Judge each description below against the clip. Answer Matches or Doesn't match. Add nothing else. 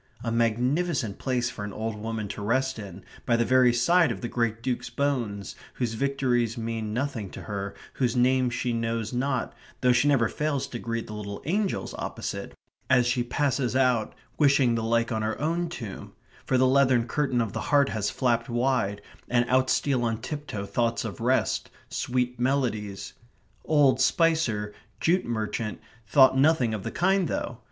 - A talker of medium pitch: Doesn't match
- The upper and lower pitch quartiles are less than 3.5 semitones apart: Matches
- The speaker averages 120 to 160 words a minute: Doesn't match